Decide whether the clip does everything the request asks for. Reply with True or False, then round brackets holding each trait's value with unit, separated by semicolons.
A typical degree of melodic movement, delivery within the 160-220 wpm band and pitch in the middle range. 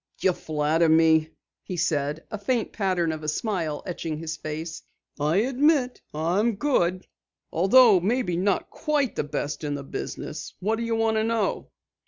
False (6.1 semitones; 165 wpm; 180 Hz)